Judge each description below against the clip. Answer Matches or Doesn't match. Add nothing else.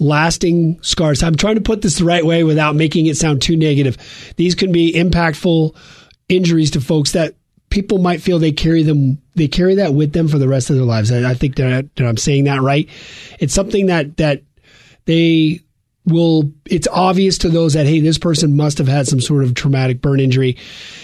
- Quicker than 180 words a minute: Matches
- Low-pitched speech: Doesn't match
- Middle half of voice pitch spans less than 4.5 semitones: Matches